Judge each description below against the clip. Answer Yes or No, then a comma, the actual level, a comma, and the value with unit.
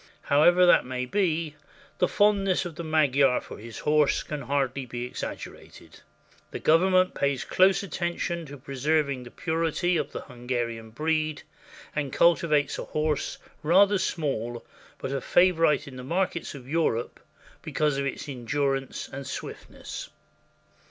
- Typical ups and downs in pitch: Yes, average, 4.1 semitones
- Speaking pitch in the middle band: Yes, medium, 150 Hz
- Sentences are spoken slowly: No, average, 145 wpm